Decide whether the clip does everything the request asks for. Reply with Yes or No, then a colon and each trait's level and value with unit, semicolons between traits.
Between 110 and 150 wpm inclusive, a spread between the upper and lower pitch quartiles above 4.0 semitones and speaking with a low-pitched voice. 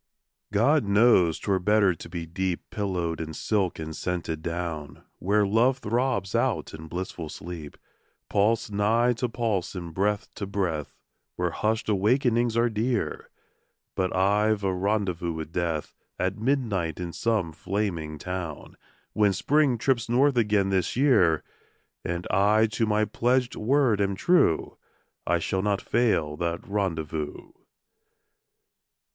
Yes: slow, 135 wpm; average, 4.6 semitones; low, 100 Hz